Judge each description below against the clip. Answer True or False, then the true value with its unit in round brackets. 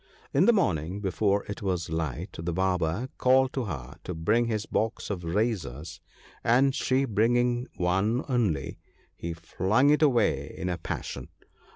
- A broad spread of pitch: True (6.2 semitones)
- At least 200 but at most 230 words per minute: False (155 wpm)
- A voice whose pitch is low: True (100 Hz)